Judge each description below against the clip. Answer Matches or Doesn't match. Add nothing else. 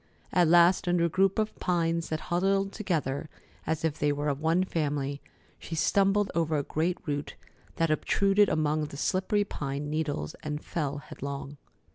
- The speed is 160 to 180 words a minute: Matches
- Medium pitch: Matches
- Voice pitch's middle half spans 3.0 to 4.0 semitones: Matches